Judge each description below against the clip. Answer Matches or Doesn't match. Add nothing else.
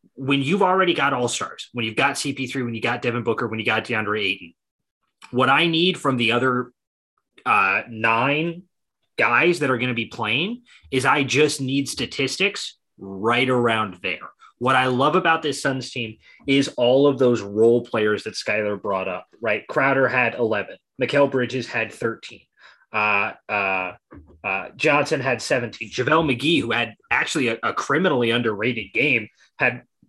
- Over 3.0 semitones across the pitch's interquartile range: Matches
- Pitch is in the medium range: Doesn't match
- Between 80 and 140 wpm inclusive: Doesn't match